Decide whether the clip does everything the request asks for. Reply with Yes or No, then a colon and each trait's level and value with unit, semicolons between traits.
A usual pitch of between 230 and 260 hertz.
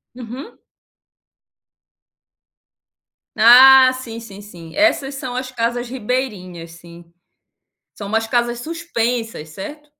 Yes: high, 240 Hz